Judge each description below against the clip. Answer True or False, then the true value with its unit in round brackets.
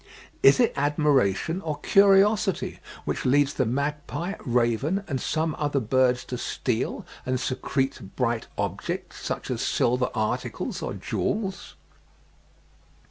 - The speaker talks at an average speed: False (120 wpm)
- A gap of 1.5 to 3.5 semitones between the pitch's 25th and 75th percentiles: False (4.5 semitones)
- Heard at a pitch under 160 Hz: True (140 Hz)